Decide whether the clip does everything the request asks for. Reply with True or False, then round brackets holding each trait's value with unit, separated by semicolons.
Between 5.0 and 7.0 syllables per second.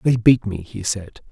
False (4.5 syllables/s)